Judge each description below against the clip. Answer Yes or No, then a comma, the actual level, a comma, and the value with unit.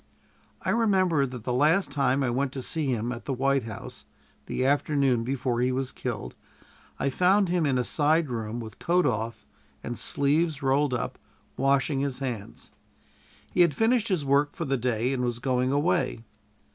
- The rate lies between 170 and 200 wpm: Yes, average, 180 wpm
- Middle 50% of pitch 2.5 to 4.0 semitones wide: Yes, average, 3.5 semitones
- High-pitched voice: No, low, 135 Hz